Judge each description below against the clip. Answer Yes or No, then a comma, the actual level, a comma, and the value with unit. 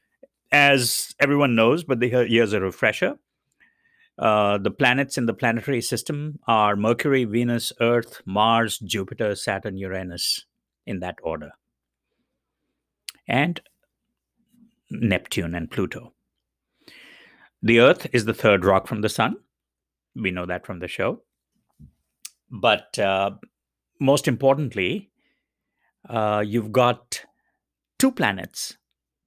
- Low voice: Yes, low, 115 Hz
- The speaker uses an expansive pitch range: Yes, wide, 5.9 semitones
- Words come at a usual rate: No, slow, 110 wpm